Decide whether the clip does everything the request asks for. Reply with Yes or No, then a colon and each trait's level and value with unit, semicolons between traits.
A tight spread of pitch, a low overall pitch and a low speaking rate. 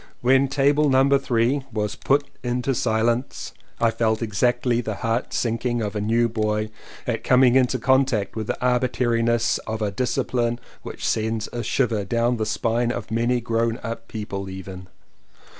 No: narrow, 2.2 semitones; low, 115 Hz; average, 160 wpm